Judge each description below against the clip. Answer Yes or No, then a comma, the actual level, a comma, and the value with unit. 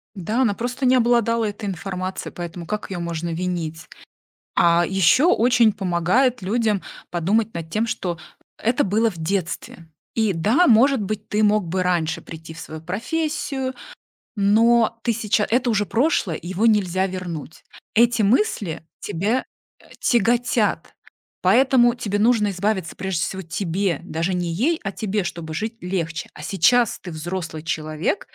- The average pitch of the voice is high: Yes, high, 200 Hz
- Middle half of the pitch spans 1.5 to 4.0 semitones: No, average, 5.0 semitones